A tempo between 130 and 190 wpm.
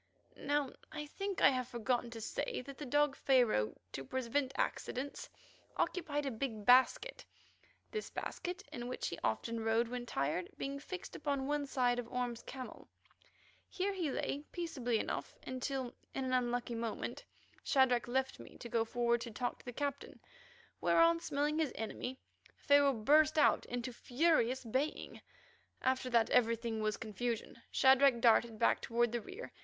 Yes: average, 160 wpm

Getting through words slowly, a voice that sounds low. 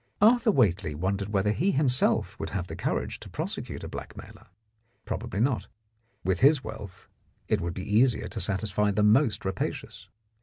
No: average, 160 wpm; low, 105 Hz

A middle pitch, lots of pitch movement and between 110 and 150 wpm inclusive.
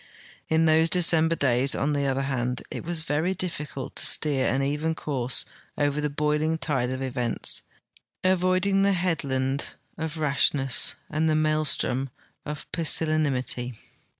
No: medium, 150 Hz; average, 3.1 semitones; average, 140 wpm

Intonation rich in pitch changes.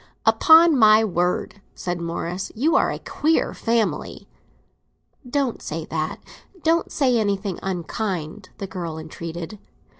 Yes: wide, 6.1 semitones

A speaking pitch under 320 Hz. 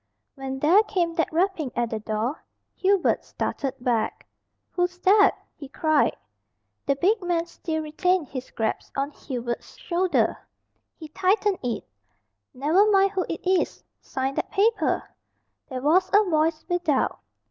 No: very high, 325 Hz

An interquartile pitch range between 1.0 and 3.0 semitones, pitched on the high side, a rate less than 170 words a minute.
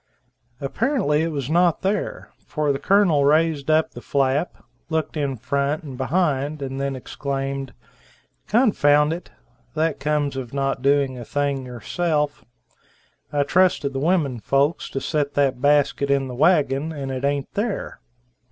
No: narrow, 2.6 semitones; medium, 145 Hz; average, 150 wpm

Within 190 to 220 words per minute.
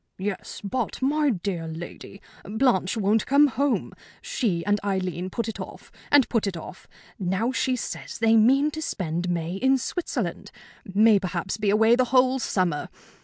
No: average, 165 wpm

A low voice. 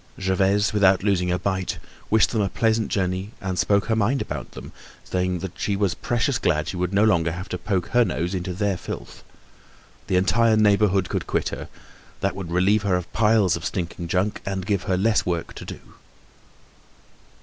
Yes: very low, 95 Hz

